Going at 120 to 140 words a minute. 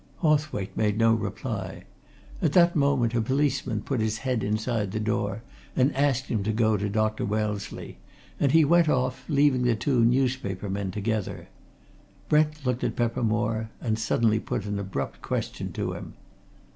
No: average, 160 wpm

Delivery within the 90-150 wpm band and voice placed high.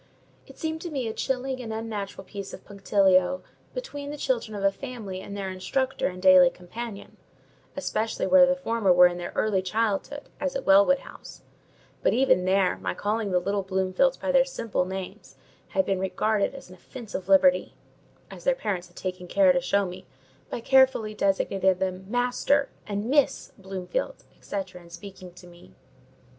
No: average, 175 wpm; high, 200 Hz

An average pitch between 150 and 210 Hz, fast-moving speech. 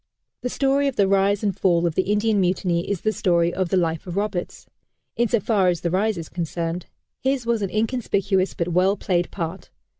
Yes: high, 190 Hz; fast, 210 wpm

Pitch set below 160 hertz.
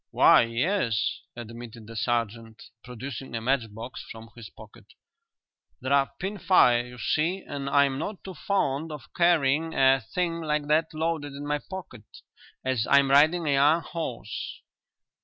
Yes: medium, 140 Hz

